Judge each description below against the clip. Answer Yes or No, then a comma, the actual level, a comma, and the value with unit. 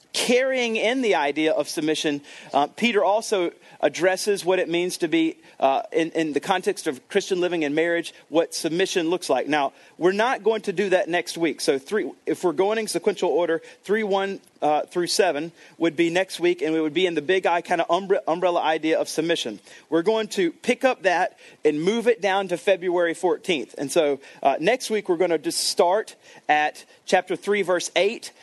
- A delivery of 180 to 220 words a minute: Yes, fast, 205 wpm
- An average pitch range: Yes, average, 4.2 semitones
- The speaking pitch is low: No, medium, 180 Hz